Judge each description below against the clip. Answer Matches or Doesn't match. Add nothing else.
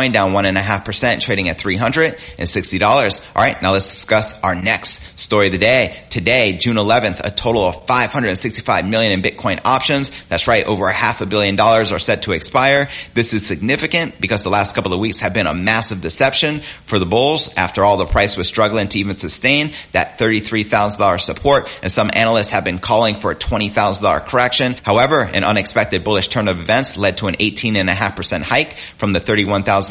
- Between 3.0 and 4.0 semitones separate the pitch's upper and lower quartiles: Matches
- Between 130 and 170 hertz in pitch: Doesn't match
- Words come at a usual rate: Doesn't match